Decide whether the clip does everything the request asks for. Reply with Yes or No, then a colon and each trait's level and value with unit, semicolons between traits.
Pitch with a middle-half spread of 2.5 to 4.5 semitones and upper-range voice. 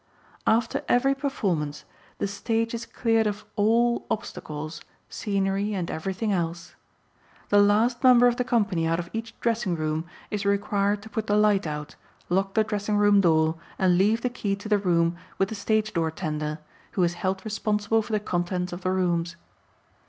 Yes: average, 4.0 semitones; high, 200 Hz